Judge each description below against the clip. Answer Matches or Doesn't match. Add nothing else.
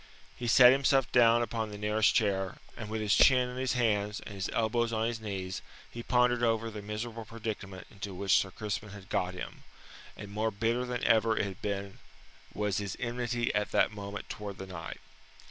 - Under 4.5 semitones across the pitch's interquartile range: Matches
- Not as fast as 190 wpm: Doesn't match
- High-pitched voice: Doesn't match